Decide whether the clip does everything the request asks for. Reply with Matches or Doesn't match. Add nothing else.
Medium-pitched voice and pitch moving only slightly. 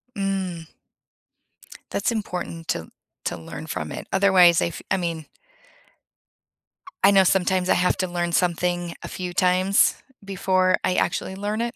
Matches